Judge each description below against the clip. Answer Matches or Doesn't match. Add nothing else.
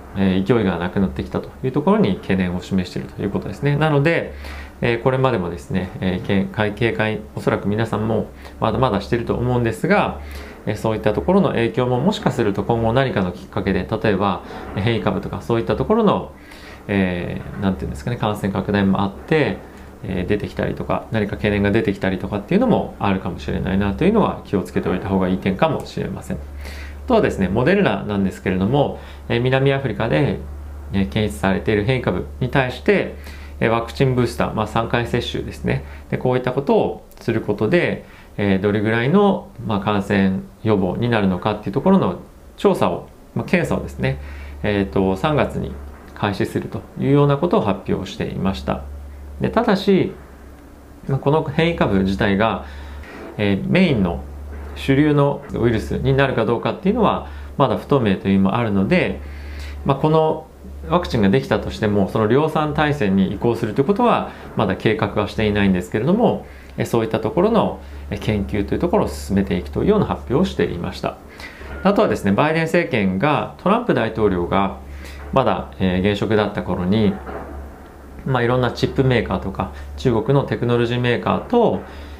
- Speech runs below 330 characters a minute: Doesn't match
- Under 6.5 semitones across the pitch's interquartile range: Matches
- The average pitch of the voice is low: Matches